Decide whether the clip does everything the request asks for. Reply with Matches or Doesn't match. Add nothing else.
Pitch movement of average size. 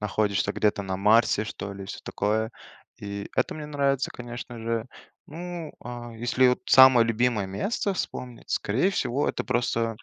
Matches